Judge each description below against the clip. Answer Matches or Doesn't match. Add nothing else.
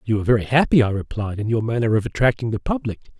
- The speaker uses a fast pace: Matches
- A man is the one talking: Matches